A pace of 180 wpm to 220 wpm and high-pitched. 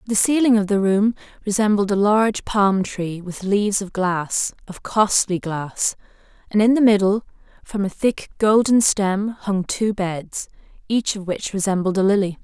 No: average, 170 wpm; high, 200 Hz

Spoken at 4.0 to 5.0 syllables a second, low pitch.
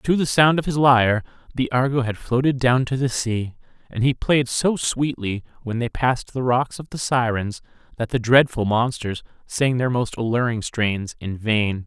Yes: 4.7 syllables/s; low, 125 Hz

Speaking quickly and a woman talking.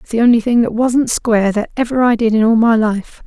Yes: fast, 275 wpm; female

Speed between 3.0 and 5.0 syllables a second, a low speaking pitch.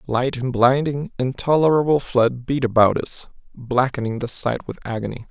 Yes: 4.8 syllables/s; low, 130 Hz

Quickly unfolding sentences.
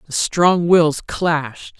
No: slow, 135 wpm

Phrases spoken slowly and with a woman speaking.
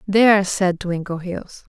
Yes: slow, 100 wpm; female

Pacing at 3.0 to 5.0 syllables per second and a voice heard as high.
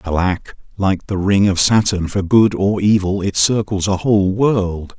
No: 4.3 syllables/s; low, 100 Hz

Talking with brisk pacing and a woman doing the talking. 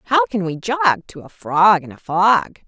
Yes: fast, 225 wpm; female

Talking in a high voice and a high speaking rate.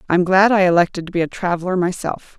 No: medium, 180 Hz; fast, 225 wpm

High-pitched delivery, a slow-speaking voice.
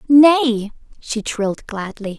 Yes: high, 235 Hz; slow, 110 wpm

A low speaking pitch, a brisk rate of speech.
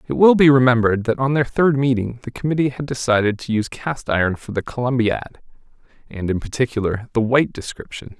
No: low, 125 Hz; average, 190 wpm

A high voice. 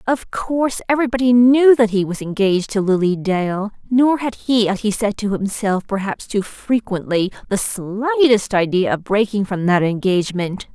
Yes: high, 210 Hz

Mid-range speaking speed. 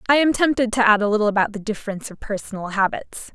No: fast, 235 wpm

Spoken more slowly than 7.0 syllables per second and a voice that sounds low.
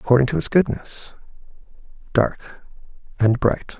Yes: 4.8 syllables/s; low, 130 Hz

